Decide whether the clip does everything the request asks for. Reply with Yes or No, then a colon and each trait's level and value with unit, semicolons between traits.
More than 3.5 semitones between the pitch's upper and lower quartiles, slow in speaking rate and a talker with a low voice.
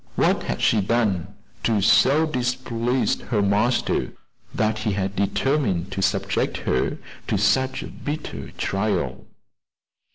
Yes: average, 4.3 semitones; slow, 125 wpm; low, 110 Hz